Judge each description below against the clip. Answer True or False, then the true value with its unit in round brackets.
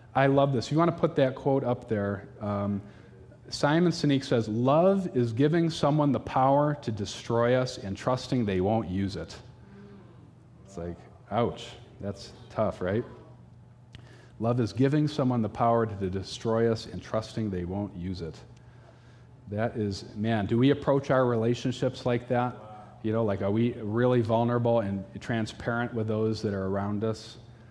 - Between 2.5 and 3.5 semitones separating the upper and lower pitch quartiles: True (3.0 semitones)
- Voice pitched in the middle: False (120 Hz)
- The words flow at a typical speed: True (165 wpm)